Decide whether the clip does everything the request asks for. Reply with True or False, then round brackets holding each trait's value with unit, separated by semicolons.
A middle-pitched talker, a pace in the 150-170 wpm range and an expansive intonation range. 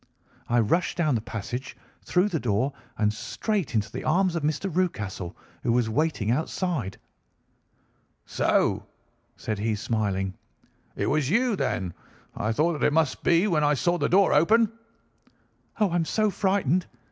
True (150 Hz; 160 wpm; 8.2 semitones)